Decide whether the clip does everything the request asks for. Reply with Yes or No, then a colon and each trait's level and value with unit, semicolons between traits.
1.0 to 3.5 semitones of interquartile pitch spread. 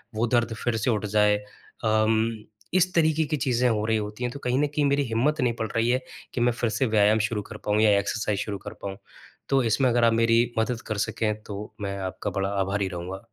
Yes: average, 2.8 semitones